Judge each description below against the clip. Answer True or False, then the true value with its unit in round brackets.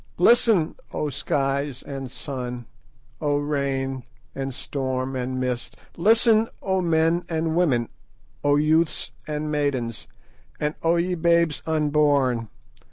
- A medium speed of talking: False (115 wpm)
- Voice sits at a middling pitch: True (145 Hz)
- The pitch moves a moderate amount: True (3.6 semitones)